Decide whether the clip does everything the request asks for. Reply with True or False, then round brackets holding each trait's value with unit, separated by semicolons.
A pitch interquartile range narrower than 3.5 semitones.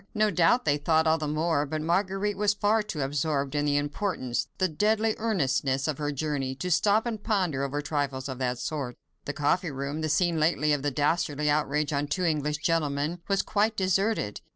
False (4.6 semitones)